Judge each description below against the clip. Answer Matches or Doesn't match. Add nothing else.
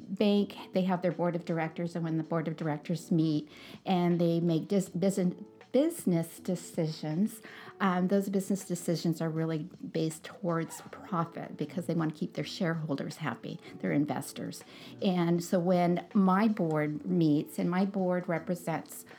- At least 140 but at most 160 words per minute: Matches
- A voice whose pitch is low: Doesn't match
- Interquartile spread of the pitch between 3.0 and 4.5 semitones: Doesn't match